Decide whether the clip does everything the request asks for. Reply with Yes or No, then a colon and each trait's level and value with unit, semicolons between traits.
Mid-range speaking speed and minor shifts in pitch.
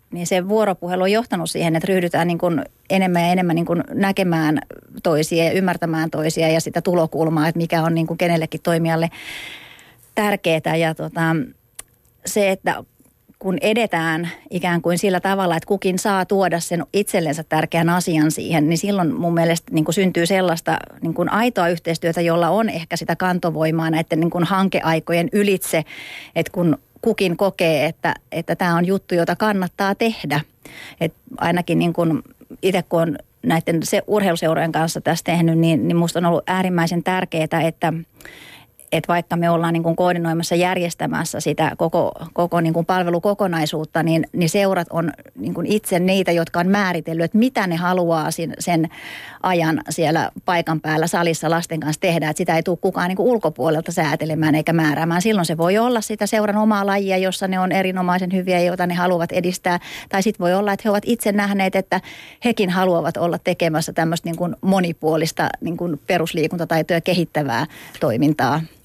No: fast, 165 wpm; narrow, 2.3 semitones